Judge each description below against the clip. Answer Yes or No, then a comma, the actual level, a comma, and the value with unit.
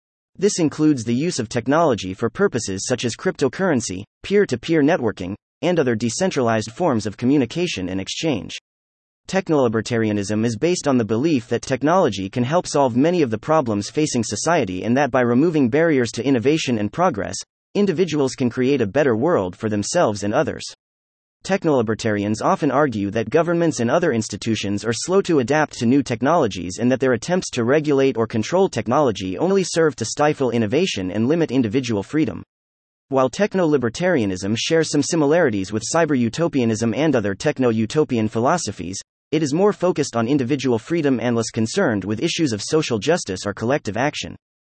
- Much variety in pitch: Yes, wide, 5.9 semitones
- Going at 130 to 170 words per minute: Yes, average, 165 wpm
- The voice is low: Yes, low, 120 Hz